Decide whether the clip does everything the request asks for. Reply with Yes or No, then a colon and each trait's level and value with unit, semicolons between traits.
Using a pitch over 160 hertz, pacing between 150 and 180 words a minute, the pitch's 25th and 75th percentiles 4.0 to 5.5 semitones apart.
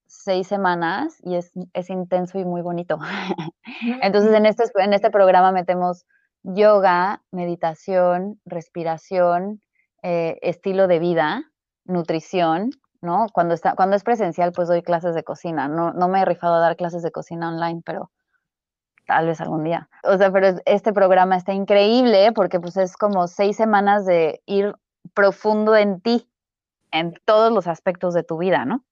No: medium, 185 Hz; average, 160 wpm; average, 2.7 semitones